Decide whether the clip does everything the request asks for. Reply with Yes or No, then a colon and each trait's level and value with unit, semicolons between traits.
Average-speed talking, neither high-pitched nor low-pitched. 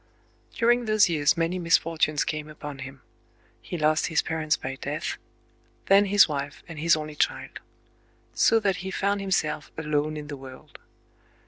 Yes: average, 150 wpm; medium, 155 Hz